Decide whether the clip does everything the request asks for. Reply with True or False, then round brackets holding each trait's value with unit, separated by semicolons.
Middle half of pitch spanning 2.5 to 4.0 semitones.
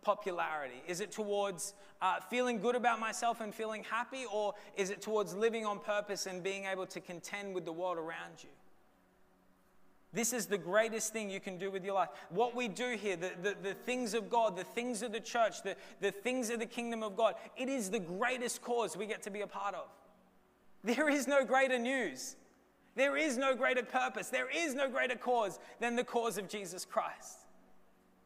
True (3.6 semitones)